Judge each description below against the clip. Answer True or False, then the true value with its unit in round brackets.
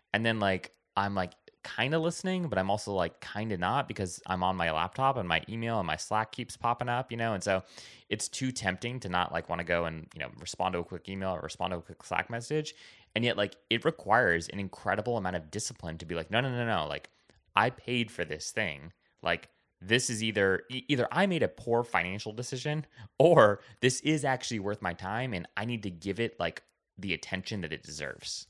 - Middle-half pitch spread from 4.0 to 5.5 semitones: True (4.8 semitones)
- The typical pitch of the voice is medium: False (105 Hz)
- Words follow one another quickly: True (235 wpm)